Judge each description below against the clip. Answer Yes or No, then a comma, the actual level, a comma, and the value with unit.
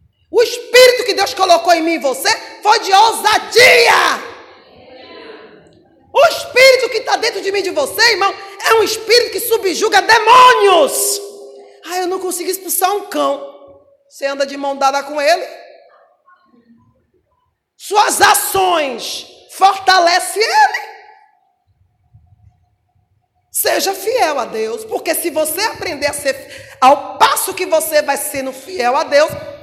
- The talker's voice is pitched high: Yes, very high, 365 Hz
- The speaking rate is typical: Yes, average, 135 wpm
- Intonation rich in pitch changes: Yes, wide, 6.8 semitones